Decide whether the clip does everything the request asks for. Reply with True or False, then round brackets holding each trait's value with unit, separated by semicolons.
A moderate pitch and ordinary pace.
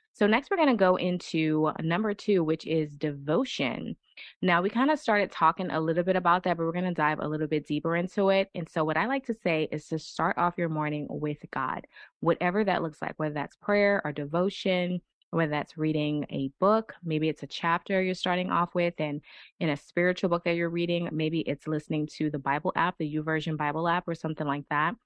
False (170 Hz; 225 wpm)